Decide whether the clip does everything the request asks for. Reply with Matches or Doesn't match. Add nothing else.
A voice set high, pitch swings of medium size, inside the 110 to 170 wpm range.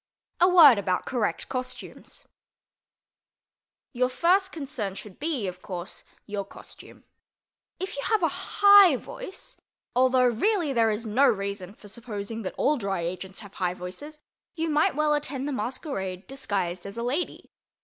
Doesn't match